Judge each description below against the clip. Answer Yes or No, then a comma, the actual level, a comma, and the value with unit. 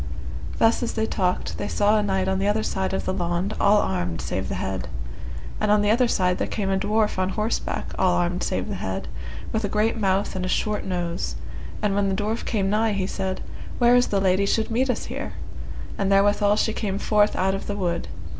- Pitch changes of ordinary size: No, narrow, 2.1 semitones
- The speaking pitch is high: Yes, high, 200 Hz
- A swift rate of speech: Yes, fast, 225 wpm